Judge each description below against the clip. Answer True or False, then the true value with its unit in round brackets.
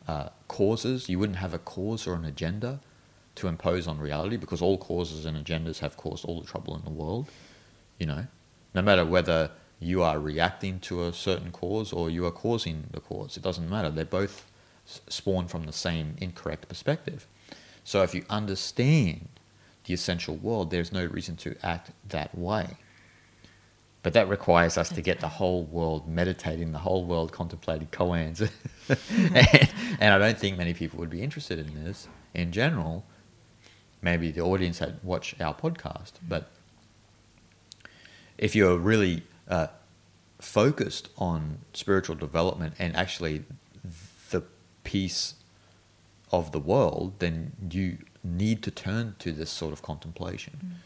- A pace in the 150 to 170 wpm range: True (155 wpm)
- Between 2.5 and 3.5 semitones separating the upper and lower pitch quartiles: False (4.0 semitones)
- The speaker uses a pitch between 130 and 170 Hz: False (90 Hz)